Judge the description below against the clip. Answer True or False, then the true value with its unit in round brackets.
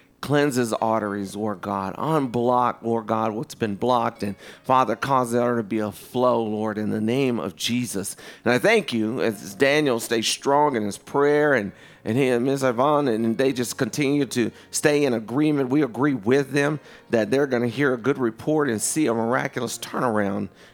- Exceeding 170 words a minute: True (195 wpm)